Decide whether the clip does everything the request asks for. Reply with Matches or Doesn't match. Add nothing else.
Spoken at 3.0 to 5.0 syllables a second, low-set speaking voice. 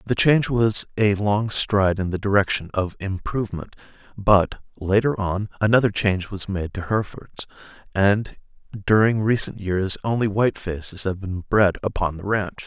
Matches